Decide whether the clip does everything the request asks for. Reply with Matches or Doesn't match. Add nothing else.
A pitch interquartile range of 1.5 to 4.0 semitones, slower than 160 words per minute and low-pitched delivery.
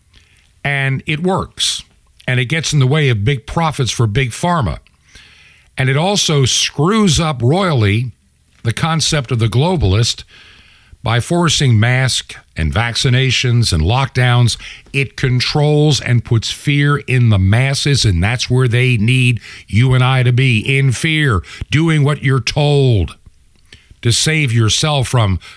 Doesn't match